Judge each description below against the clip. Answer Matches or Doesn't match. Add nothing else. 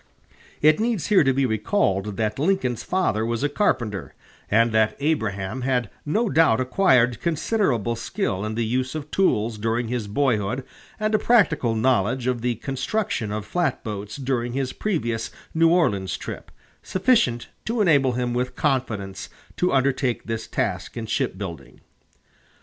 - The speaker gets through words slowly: Doesn't match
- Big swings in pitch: Matches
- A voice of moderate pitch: Doesn't match